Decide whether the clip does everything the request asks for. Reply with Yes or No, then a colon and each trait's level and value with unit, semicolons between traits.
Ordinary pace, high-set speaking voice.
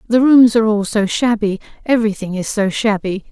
Yes: average, 165 wpm; high, 215 Hz